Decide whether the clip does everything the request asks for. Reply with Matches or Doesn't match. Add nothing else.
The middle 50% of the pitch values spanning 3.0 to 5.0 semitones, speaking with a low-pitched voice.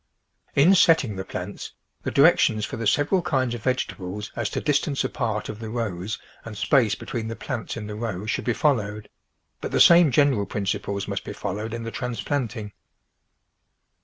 Matches